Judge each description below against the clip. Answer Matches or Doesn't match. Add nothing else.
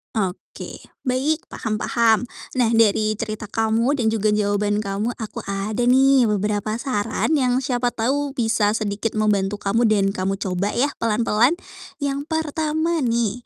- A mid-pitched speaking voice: Doesn't match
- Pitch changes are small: Doesn't match